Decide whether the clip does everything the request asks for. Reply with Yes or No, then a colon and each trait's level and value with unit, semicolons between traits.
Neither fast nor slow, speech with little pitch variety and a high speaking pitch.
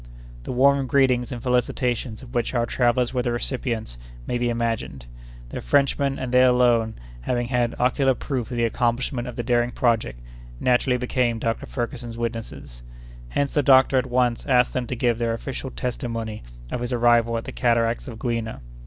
No: average, 180 wpm; narrow, 1.5 semitones; low, 120 Hz